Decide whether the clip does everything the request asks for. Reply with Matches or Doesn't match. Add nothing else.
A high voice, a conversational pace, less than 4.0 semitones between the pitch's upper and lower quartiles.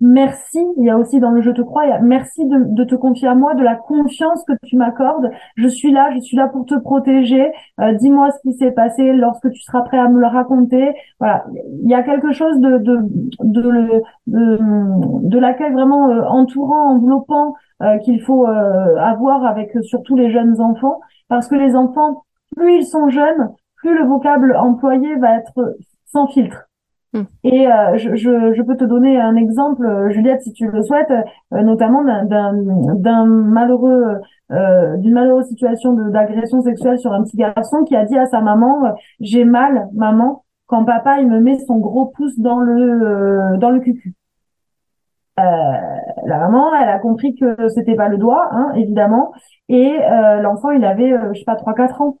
Matches